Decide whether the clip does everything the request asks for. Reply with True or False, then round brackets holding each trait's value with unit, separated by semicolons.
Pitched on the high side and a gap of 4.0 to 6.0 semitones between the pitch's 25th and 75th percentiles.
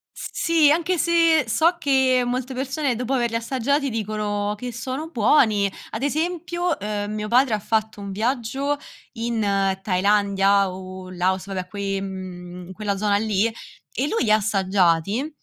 True (220 Hz; 5.2 semitones)